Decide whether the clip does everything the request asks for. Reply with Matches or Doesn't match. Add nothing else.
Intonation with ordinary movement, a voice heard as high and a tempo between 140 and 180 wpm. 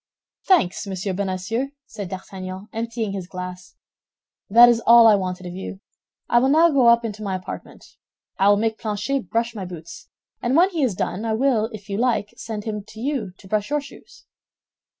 Doesn't match